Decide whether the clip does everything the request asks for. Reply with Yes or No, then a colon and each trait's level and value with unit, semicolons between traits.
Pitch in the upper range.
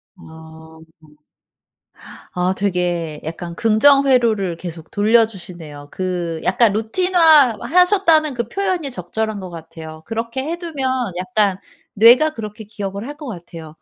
Yes: high, 210 Hz